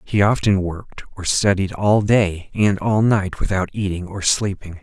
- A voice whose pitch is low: Yes, low, 100 Hz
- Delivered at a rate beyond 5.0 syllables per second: No, 4.4 syllables/s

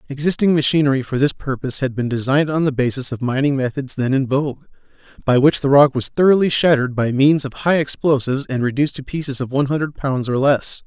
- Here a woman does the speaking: No, male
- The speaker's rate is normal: No, fast, 215 wpm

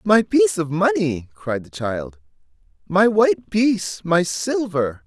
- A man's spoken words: Yes, male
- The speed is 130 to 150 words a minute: Yes, average, 140 wpm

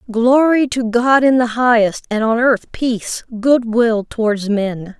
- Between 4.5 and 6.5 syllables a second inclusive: No, 4.0 syllables/s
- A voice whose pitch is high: Yes, high, 235 Hz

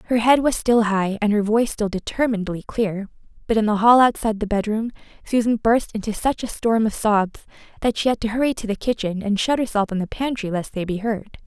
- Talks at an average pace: No, fast, 225 wpm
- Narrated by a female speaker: Yes, female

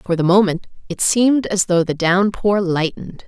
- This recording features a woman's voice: Yes, female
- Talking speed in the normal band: Yes, average, 185 wpm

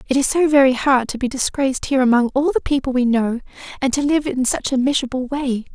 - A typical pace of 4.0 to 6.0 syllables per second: No, 6.3 syllables/s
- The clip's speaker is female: Yes, female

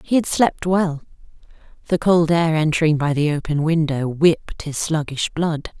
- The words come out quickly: No, average, 165 wpm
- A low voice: No, medium, 160 Hz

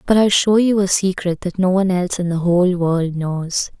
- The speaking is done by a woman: Yes, female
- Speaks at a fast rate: Yes, fast, 235 wpm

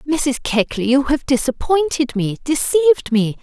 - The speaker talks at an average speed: No, slow, 125 wpm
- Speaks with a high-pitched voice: Yes, very high, 250 Hz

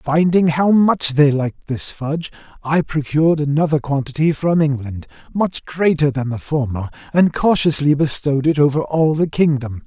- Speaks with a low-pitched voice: No, medium, 150 Hz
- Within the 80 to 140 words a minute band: No, average, 160 wpm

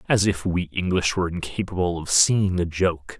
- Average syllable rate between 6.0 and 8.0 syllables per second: No, 5.0 syllables/s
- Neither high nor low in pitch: No, very low, 90 Hz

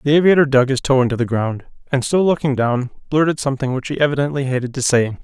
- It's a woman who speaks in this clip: No, male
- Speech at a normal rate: No, fast, 230 wpm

